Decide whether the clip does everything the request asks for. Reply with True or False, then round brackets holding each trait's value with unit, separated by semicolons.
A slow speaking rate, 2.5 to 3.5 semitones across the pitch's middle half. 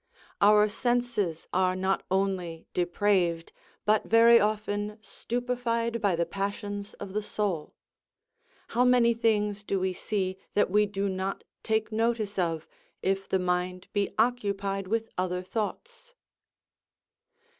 True (125 wpm; 3.1 semitones)